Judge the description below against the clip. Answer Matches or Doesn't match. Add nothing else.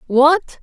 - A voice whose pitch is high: Matches